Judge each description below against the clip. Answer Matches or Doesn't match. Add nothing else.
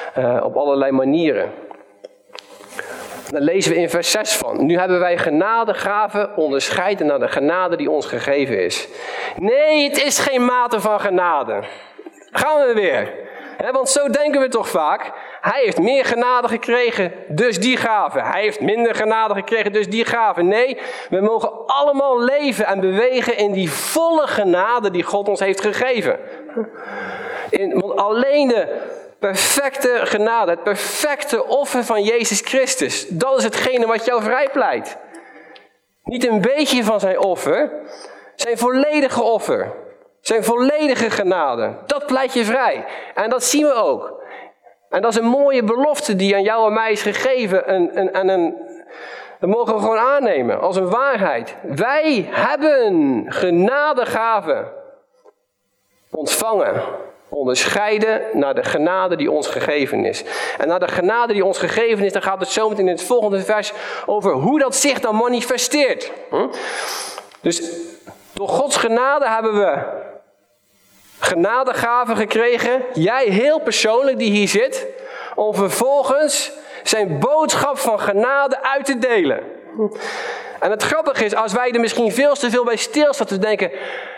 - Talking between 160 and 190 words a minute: Doesn't match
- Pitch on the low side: Doesn't match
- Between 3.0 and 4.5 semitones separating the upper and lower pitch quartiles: Doesn't match